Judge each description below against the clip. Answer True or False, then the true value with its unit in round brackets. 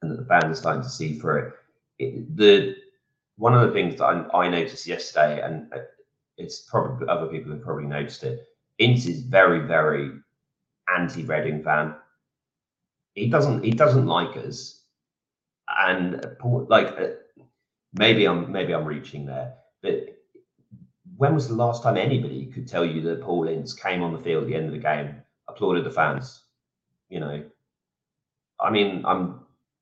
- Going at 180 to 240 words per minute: False (165 wpm)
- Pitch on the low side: True (115 Hz)